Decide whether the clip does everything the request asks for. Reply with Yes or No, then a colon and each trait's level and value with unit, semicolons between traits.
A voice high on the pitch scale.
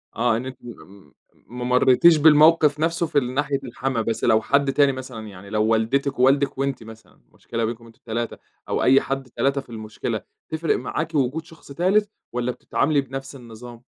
No: low, 130 Hz